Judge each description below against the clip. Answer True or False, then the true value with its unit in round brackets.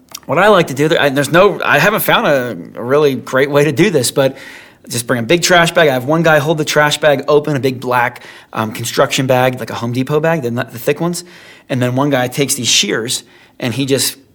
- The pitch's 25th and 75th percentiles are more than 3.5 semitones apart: False (3.2 semitones)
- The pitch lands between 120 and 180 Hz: True (135 Hz)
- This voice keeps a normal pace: False (245 wpm)